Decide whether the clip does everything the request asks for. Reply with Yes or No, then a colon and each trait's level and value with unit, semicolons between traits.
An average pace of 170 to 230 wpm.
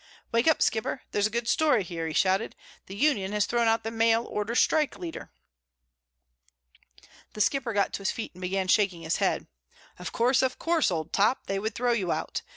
Yes: average, 200 wpm